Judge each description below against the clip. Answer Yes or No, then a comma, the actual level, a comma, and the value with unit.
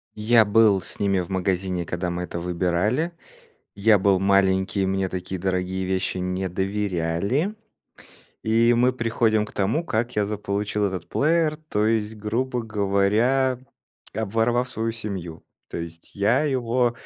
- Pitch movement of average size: Yes, average, 3.6 semitones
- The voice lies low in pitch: Yes, low, 105 Hz